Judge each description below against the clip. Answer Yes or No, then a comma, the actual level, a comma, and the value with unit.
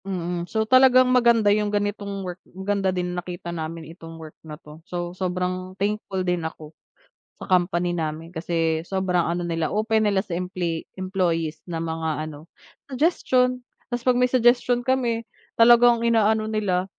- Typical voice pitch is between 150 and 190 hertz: Yes, medium, 185 Hz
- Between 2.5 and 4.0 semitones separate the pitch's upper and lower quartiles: No, average, 4.5 semitones